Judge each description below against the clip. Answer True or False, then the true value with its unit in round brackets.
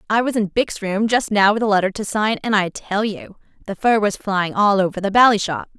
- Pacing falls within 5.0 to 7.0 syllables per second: True (5.4 syllables/s)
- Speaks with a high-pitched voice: True (205 Hz)